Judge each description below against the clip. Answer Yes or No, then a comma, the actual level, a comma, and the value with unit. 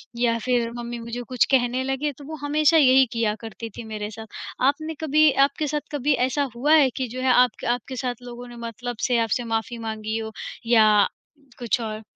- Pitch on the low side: No, high, 245 Hz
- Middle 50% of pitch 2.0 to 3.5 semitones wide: Yes, average, 2.9 semitones